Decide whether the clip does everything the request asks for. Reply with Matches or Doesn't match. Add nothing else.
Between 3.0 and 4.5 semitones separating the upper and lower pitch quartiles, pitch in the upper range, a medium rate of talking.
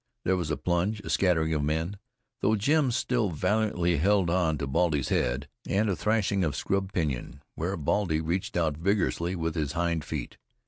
Doesn't match